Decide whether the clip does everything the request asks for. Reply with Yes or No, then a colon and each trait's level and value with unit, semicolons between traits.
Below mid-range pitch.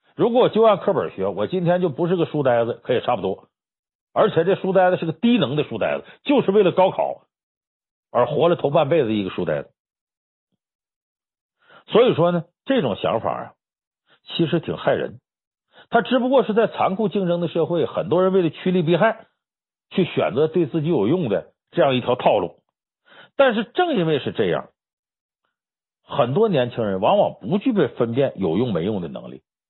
No: medium, 180 Hz